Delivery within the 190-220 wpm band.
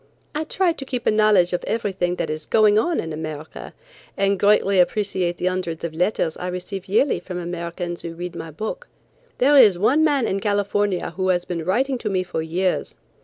Yes: average, 200 wpm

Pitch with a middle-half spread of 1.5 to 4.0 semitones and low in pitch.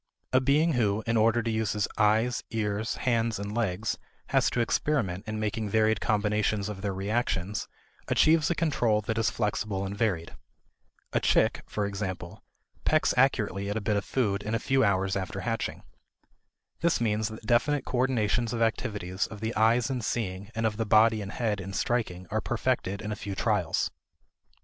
Yes: narrow, 2.5 semitones; low, 110 Hz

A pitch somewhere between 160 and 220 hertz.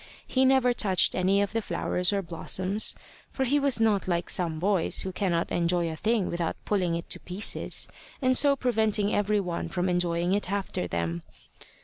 Yes: high, 190 Hz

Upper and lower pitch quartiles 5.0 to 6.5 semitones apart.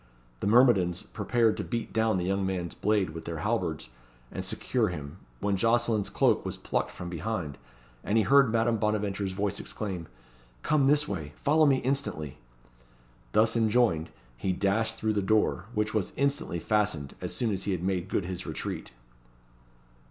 No: average, 4.1 semitones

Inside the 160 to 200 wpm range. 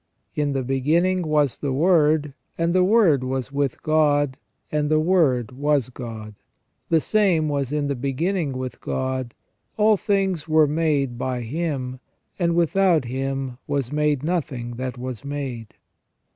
No: average, 150 wpm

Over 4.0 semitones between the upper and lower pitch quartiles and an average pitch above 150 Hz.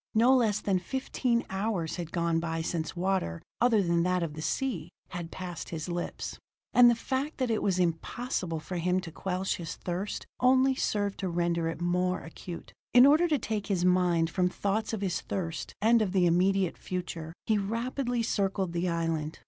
Yes: average, 4.5 semitones; medium, 185 Hz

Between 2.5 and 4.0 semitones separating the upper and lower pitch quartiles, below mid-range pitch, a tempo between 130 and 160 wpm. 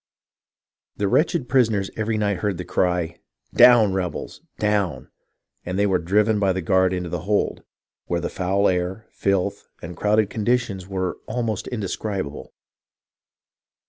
Yes: average, 2.8 semitones; low, 100 Hz; average, 145 wpm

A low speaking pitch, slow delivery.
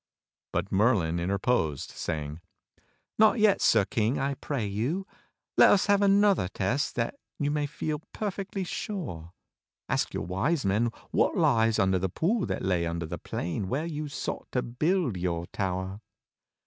No: low, 115 Hz; average, 160 wpm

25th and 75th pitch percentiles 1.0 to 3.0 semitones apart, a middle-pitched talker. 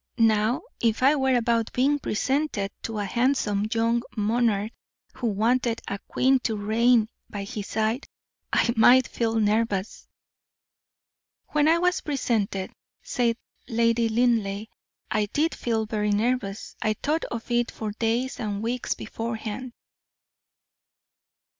No: average, 2.7 semitones; high, 230 Hz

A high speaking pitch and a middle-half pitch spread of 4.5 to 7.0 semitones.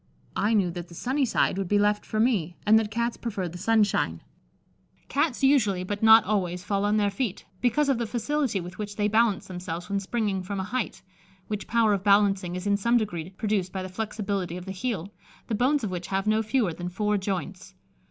No: high, 205 Hz; average, 3.1 semitones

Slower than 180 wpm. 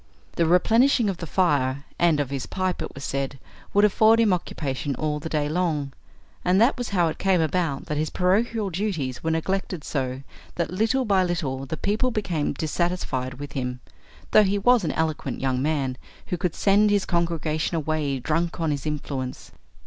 No: average, 185 wpm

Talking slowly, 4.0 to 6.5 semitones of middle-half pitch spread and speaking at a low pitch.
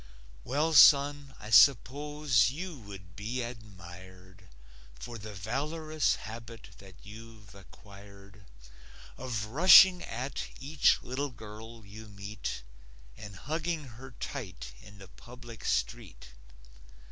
Yes: slow, 110 wpm; wide, 5.6 semitones; low, 115 Hz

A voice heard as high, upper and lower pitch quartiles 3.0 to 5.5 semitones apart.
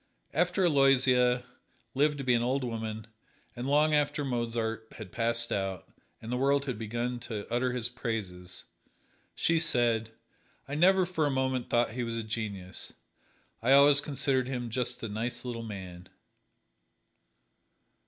No: low, 125 Hz; average, 3.4 semitones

